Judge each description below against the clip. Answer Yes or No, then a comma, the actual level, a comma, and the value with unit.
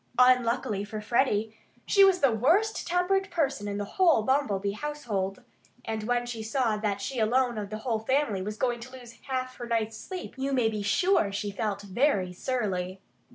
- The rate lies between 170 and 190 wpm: Yes, average, 185 wpm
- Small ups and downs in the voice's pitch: No, average, 4.3 semitones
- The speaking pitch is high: Yes, high, 235 Hz